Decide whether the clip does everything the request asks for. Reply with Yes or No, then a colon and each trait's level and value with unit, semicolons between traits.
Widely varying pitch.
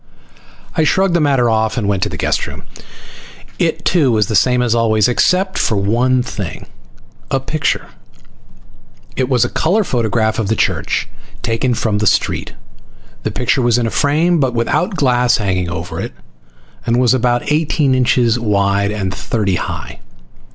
No: average, 3.7 semitones